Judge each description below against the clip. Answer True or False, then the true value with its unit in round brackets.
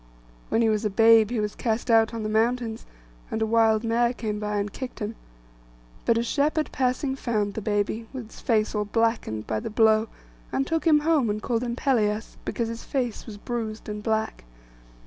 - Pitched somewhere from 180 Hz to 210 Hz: False (225 Hz)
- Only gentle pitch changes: True (2.1 semitones)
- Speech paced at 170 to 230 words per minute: True (205 wpm)